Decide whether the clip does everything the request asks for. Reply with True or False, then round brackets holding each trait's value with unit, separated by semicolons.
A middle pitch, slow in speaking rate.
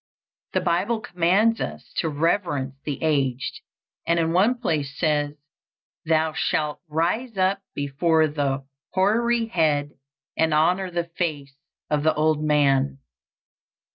True (160 Hz; 125 wpm)